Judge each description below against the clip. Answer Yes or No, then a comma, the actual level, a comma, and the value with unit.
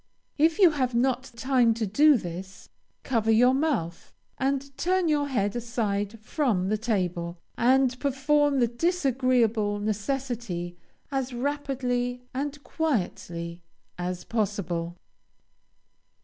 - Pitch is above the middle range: Yes, high, 245 Hz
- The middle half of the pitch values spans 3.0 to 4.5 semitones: No, average, 4.9 semitones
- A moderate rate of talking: No, slow, 110 wpm